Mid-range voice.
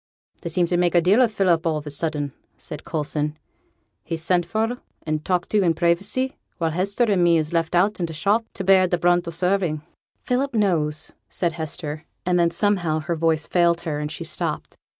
Yes: medium, 170 Hz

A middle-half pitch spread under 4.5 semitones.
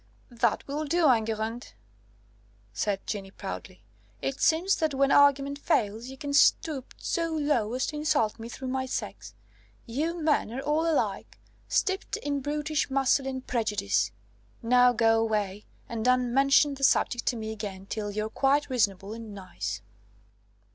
No: average, 4.8 semitones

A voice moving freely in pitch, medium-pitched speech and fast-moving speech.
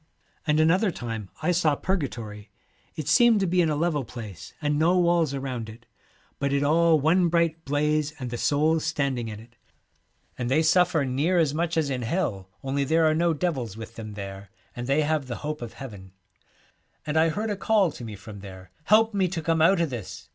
Yes: wide, 5.7 semitones; medium, 150 Hz; fast, 225 wpm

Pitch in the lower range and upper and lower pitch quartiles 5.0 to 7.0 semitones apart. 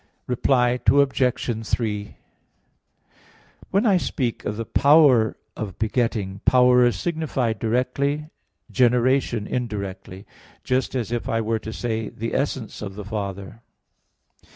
No: low, 120 Hz; average, 3.2 semitones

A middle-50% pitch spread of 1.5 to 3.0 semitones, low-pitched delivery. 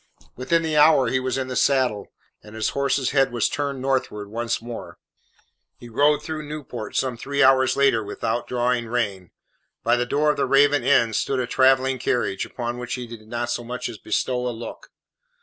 Yes: narrow, 2.6 semitones; low, 125 Hz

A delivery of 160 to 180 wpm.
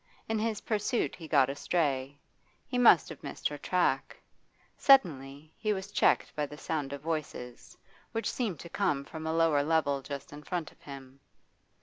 Yes: average, 175 wpm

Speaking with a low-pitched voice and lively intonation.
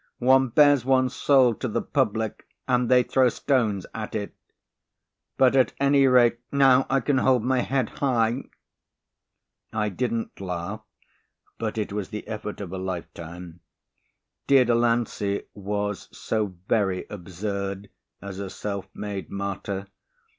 No: low, 110 Hz; average, 4.5 semitones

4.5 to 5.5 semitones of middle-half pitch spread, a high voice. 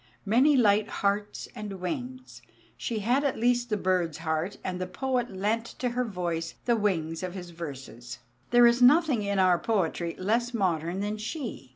Yes: average, 5.2 semitones; high, 205 Hz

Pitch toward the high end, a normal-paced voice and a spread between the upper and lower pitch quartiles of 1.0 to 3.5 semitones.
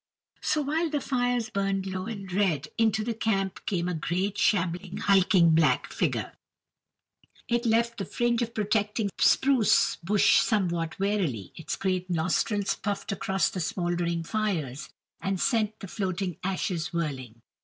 No: high, 195 Hz; average, 145 wpm; average, 4.0 semitones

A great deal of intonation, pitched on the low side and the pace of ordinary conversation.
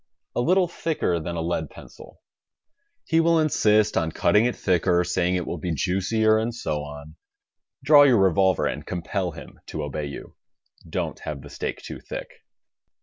Yes: wide, 6.1 semitones; very low, 90 Hz; average, 170 wpm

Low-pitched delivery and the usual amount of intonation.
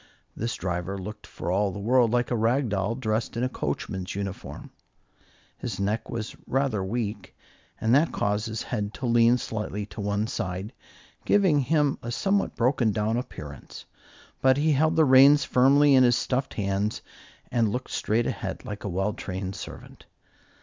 Yes: low, 115 Hz; average, 4.1 semitones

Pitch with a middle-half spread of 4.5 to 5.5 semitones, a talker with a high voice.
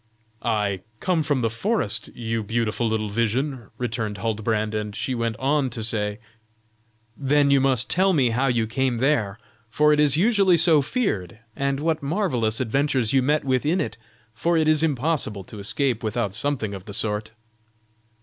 No: average, 5.2 semitones; low, 125 Hz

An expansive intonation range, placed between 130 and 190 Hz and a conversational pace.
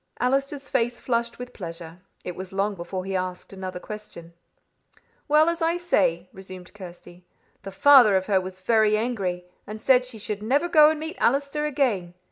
No: wide, 6.4 semitones; high, 210 Hz; average, 175 wpm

